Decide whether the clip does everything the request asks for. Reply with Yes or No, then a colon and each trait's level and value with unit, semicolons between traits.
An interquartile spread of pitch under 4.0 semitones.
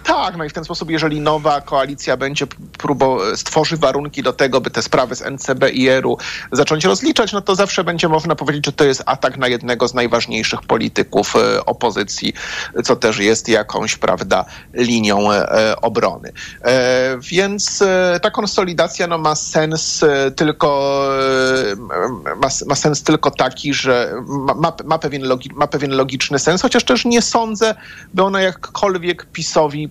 No: average, 4.6 semitones